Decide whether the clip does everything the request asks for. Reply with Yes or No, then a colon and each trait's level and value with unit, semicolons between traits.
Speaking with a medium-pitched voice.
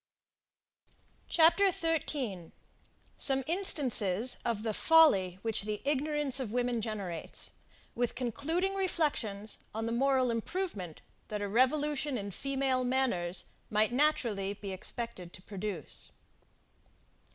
No: high, 245 Hz